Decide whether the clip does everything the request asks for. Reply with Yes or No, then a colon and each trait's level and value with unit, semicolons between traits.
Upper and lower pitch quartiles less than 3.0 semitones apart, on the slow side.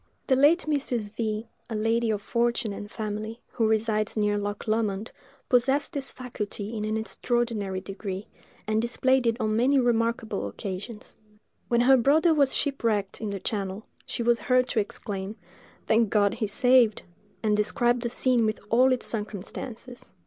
No: narrow, 2.6 semitones; average, 165 wpm